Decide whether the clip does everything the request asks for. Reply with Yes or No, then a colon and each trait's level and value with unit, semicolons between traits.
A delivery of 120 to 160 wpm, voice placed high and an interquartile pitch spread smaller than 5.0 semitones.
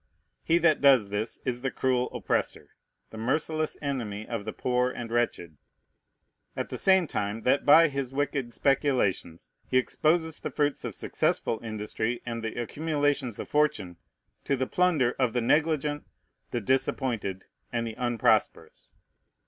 No: average, 150 wpm; low, 125 Hz; average, 4.3 semitones